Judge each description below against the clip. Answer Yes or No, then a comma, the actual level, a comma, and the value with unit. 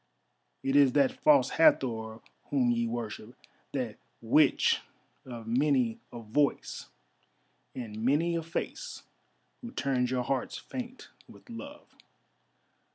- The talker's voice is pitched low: Yes, low, 130 Hz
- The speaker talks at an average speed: No, slow, 115 wpm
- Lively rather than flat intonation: No, average, 4.0 semitones